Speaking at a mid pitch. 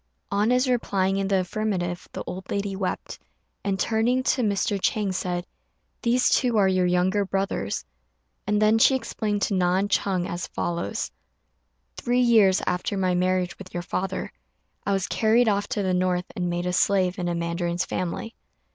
No: high, 195 Hz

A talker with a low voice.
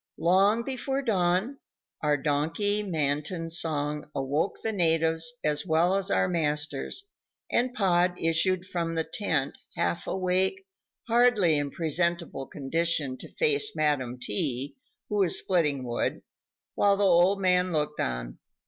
No: medium, 170 Hz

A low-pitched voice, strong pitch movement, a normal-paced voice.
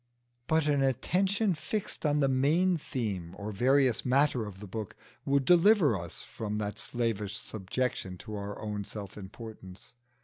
Yes: low, 120 Hz; wide, 6.0 semitones; average, 150 wpm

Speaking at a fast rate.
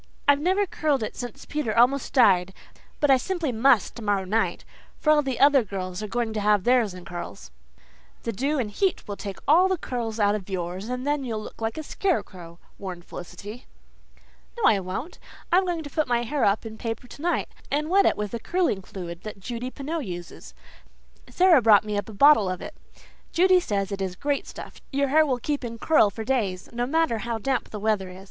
Yes: fast, 210 wpm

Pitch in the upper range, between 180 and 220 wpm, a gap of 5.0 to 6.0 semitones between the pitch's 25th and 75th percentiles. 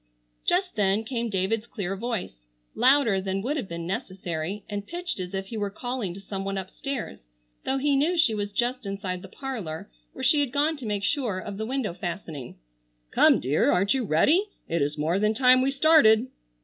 Yes: high, 210 Hz; average, 200 wpm; wide, 5.6 semitones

